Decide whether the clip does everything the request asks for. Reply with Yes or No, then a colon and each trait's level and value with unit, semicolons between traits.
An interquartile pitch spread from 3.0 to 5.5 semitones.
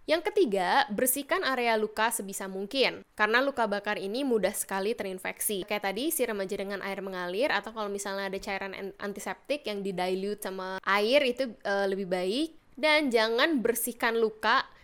Yes: average, 3.8 semitones